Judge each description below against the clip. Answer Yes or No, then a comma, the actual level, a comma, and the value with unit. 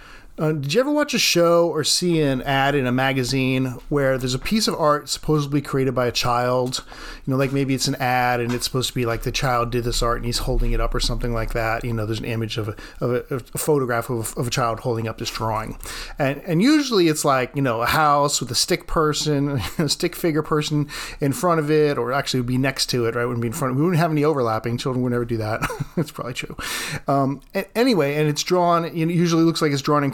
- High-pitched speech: No, low, 135 Hz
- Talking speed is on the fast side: Yes, fast, 270 wpm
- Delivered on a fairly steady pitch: No, average, 4.0 semitones